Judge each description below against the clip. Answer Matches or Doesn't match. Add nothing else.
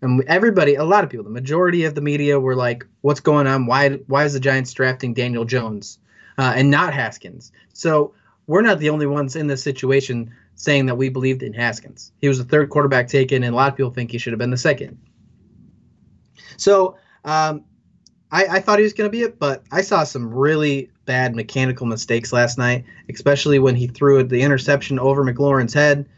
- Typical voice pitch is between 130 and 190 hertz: Matches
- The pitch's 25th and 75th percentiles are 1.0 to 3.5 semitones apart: Matches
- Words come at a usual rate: Doesn't match